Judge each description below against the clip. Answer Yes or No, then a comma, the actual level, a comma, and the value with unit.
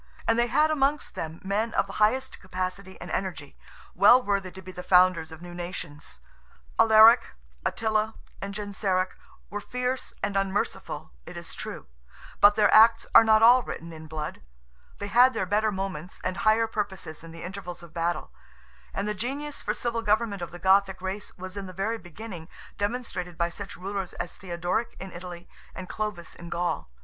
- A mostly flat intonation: No, average, 3.7 semitones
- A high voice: Yes, high, 195 Hz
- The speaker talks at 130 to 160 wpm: No, average, 180 wpm